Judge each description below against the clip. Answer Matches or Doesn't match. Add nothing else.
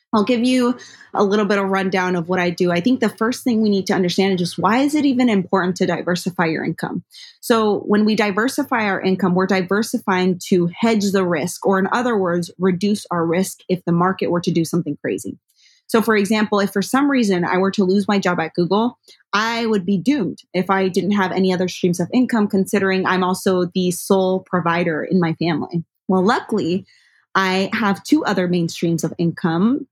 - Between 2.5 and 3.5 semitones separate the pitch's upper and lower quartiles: Matches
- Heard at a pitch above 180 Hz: Matches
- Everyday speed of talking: Doesn't match